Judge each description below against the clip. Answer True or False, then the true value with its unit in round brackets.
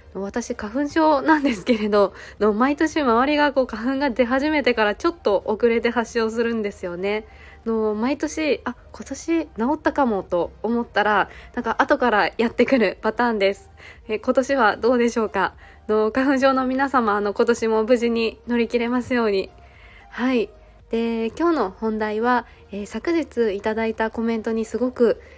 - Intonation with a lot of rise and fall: False (3.4 semitones)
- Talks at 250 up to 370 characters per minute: True (320 characters per minute)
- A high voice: True (235 Hz)